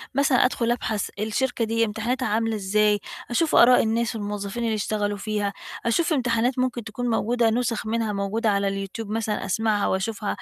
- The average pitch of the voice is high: Yes, high, 225 Hz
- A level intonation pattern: Yes, narrow, 2.3 semitones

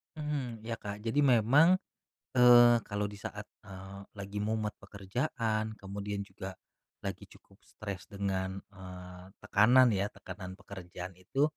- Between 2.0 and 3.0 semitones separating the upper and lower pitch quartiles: No, average, 3.4 semitones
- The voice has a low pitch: Yes, low, 105 Hz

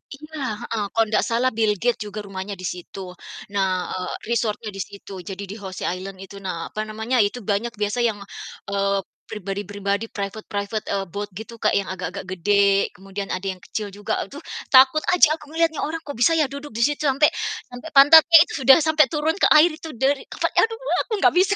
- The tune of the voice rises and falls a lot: Yes, wide, 6.1 semitones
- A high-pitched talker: Yes, high, 215 Hz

